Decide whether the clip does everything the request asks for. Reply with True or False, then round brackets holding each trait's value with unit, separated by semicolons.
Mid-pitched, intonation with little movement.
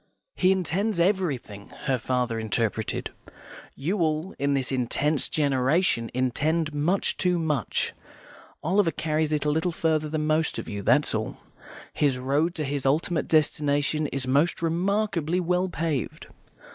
False (155 Hz; 3.8 semitones)